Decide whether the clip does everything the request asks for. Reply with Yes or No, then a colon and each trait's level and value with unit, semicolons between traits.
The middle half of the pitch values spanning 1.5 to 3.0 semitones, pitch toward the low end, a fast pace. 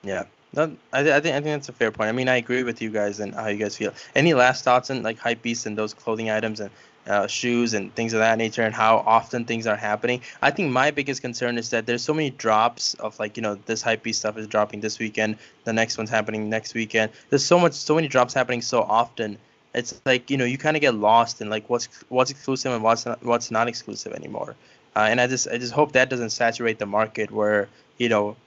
Yes: narrow, 2.5 semitones; low, 115 Hz; fast, 250 wpm